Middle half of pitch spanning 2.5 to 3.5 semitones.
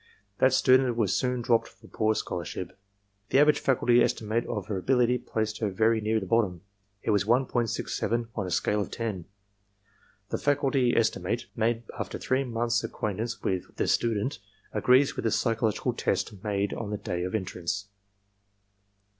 Yes: average, 3.0 semitones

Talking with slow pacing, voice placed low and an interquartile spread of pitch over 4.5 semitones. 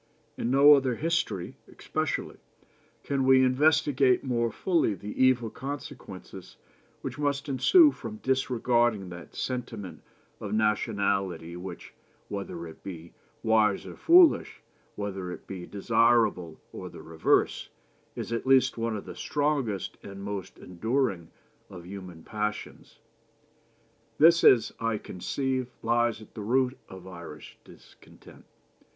Yes: slow, 125 wpm; low, 115 Hz; average, 5.3 semitones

